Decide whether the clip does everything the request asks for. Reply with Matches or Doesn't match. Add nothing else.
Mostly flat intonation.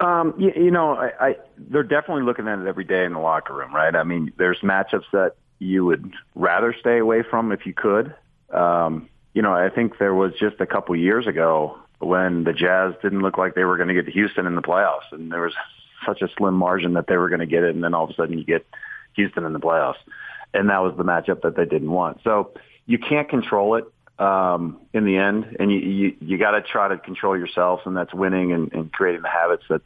Doesn't match